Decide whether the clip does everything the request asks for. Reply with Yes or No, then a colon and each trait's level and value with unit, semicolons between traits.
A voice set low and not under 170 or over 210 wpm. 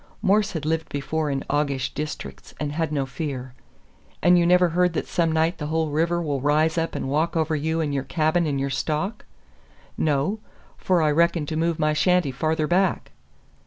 No: medium, 160 Hz; average, 195 wpm